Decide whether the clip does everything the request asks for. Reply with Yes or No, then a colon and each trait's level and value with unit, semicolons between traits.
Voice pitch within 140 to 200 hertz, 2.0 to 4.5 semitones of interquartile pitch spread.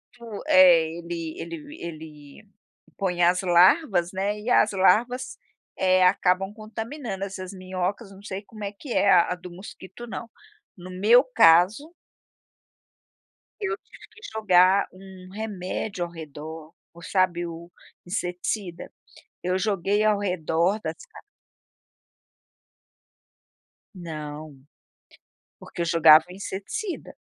Yes: medium, 185 Hz; average, 3.3 semitones